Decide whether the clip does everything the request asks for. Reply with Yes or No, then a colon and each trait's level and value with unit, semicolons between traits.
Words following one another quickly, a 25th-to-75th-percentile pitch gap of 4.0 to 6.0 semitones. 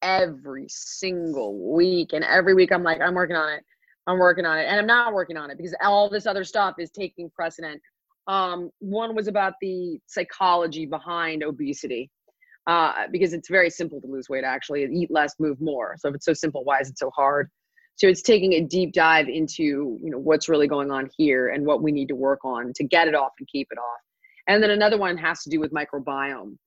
Yes: fast, 225 wpm; average, 4.3 semitones